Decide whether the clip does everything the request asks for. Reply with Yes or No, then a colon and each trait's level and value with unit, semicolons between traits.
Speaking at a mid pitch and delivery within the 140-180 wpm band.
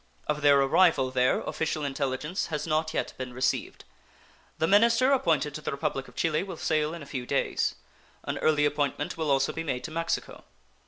No: medium, 150 Hz; average, 190 wpm